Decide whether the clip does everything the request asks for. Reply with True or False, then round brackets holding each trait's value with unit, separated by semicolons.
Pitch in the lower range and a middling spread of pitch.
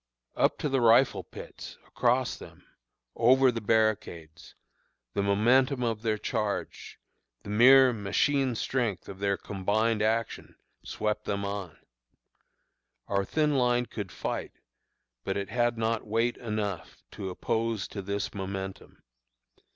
True (110 Hz; 3.3 semitones)